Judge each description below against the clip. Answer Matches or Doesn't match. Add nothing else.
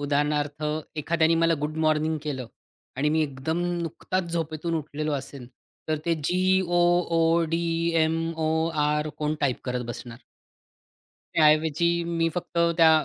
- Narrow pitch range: Matches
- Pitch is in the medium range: Matches